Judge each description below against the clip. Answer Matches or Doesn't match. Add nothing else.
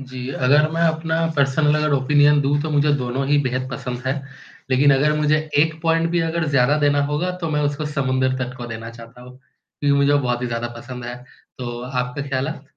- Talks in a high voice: Doesn't match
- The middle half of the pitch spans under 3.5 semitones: Matches